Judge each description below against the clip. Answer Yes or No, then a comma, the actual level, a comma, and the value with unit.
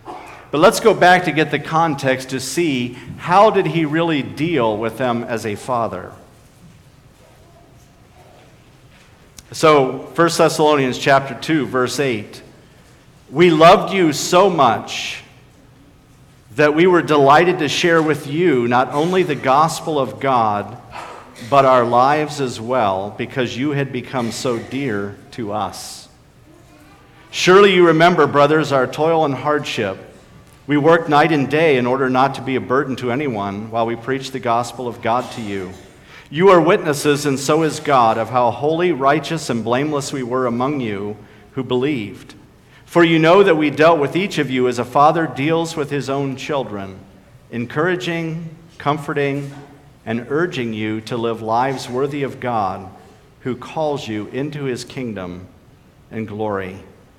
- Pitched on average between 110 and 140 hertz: Yes, low, 135 Hz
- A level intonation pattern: No, average, 4.2 semitones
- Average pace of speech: Yes, average, 155 wpm